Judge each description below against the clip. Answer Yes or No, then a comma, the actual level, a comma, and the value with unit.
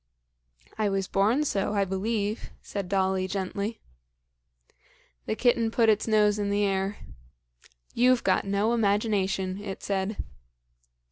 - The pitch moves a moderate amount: No, narrow, 2.0 semitones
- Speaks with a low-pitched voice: No, high, 205 Hz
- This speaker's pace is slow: Yes, slow, 125 wpm